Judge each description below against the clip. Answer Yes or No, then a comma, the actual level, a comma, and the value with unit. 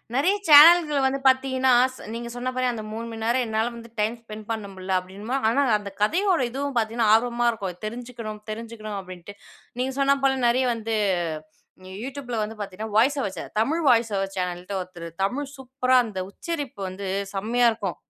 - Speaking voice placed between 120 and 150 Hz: No, high, 230 Hz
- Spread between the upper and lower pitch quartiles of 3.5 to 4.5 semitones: Yes, average, 3.9 semitones